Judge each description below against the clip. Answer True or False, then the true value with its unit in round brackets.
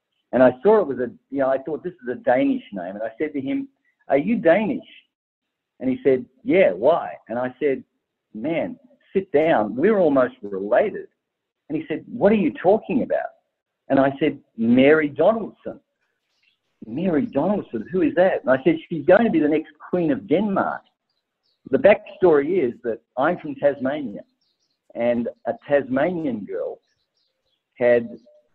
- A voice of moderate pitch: True (175 Hz)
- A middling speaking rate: True (170 wpm)